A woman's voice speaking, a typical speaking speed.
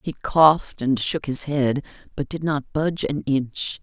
Yes: female; average, 190 wpm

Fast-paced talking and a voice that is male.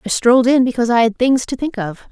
No: fast, 285 wpm; female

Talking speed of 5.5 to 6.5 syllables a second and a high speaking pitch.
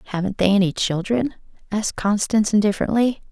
Yes: 6.3 syllables/s; high, 205 Hz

